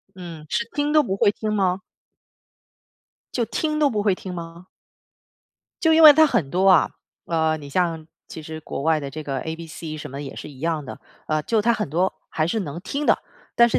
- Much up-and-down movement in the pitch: Yes, wide, 6.0 semitones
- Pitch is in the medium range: Yes, medium, 170 Hz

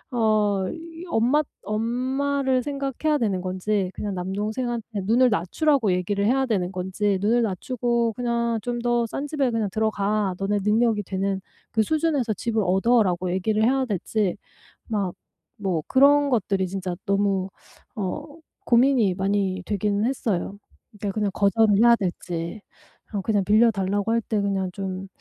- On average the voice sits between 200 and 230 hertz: Yes, high, 215 Hz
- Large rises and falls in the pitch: No, average, 3.6 semitones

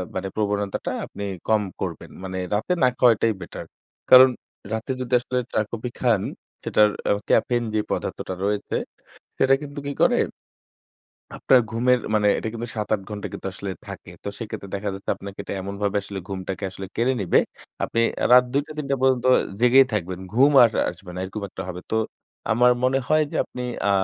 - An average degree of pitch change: Yes, average, 4.1 semitones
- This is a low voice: Yes, low, 110 Hz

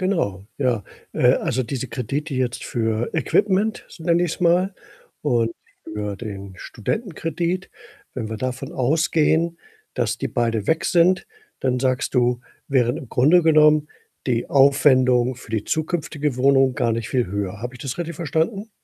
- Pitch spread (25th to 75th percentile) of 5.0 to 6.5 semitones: Yes, average, 5.3 semitones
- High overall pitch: No, low, 135 Hz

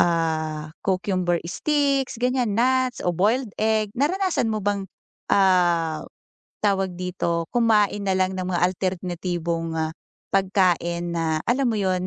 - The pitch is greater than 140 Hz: Yes, high, 190 Hz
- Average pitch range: Yes, average, 4.2 semitones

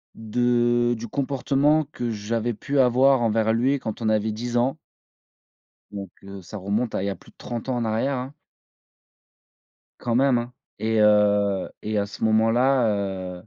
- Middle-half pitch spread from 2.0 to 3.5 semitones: Yes, average, 2.8 semitones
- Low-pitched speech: Yes, low, 115 Hz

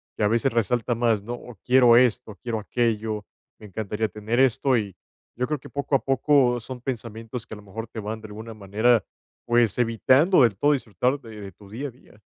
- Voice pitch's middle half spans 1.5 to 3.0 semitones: Yes, narrow, 2.6 semitones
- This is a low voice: Yes, low, 115 Hz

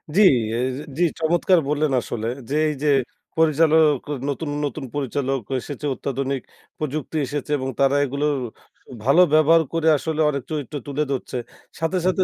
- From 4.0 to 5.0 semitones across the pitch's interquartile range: No, average, 2.7 semitones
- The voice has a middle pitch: Yes, medium, 145 Hz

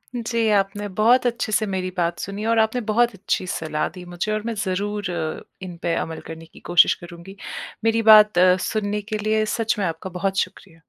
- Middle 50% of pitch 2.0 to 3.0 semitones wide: No, average, 3.5 semitones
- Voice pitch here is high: Yes, high, 200 Hz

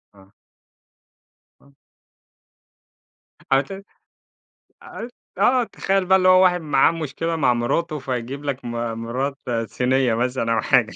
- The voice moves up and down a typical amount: No, wide, 6.1 semitones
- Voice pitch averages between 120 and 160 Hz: Yes, medium, 140 Hz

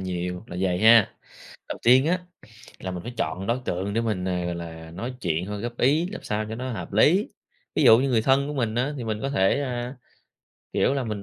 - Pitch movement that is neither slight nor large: No, wide, 5.7 semitones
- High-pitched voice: No, low, 110 Hz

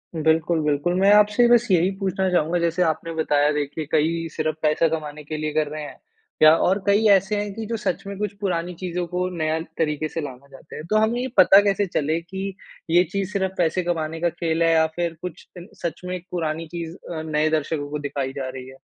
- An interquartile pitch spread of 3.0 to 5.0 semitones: Yes, average, 3.4 semitones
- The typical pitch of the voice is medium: Yes, medium, 165 Hz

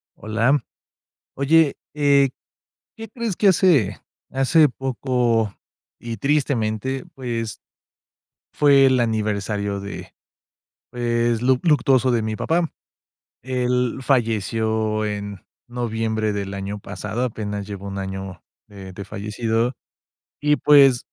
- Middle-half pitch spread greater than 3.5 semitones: Yes, average, 4.1 semitones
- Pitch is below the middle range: Yes, low, 115 Hz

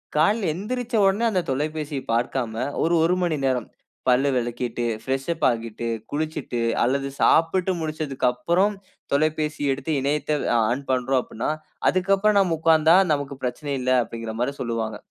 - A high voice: No, medium, 145 Hz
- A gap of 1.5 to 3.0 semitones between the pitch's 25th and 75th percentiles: No, average, 4.7 semitones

